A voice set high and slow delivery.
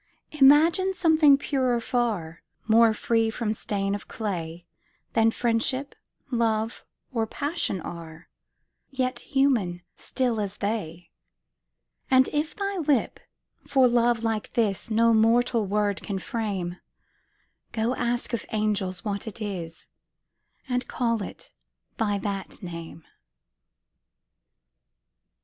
Yes: high, 225 Hz; slow, 110 wpm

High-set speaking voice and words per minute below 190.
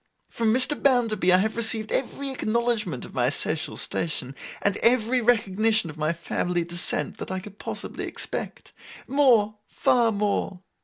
Yes: high, 215 Hz; average, 150 wpm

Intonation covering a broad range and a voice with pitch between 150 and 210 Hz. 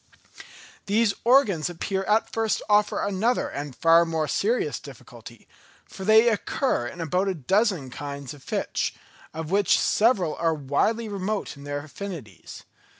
Yes: wide, 6.0 semitones; medium, 185 Hz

